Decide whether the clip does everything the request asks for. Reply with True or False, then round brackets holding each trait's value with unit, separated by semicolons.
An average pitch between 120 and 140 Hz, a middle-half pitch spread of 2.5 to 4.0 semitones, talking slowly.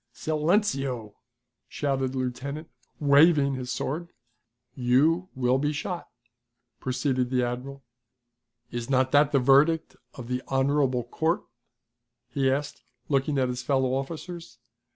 True (135 Hz; 2.8 semitones; 120 wpm)